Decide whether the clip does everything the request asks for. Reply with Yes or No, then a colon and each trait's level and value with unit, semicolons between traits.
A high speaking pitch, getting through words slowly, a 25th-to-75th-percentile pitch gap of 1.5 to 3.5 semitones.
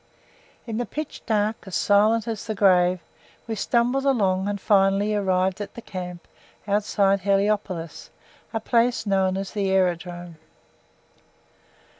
Yes: high, 200 Hz; slow, 130 wpm; average, 2.7 semitones